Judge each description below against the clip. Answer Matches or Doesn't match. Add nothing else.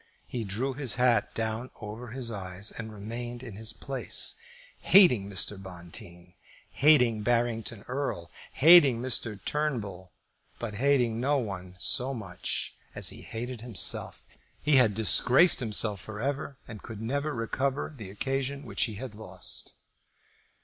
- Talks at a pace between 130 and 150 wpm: Matches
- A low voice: Matches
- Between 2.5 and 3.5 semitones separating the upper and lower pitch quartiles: Doesn't match